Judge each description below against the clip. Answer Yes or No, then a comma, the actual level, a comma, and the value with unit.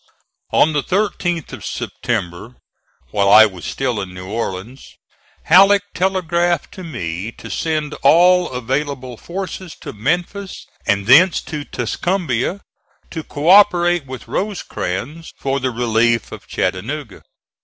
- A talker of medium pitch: Yes, medium, 145 Hz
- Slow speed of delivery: Yes, slow, 125 wpm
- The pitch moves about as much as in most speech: No, wide, 7.4 semitones